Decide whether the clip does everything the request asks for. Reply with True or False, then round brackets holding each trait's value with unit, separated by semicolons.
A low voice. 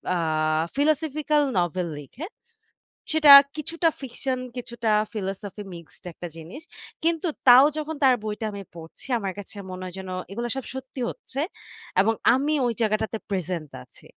False (235 Hz)